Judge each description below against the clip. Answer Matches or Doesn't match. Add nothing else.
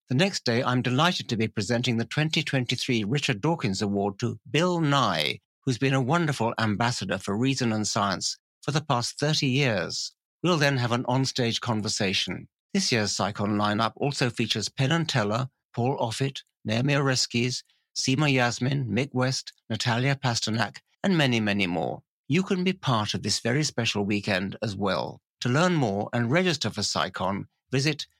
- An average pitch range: Matches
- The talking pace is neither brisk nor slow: Matches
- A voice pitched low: Matches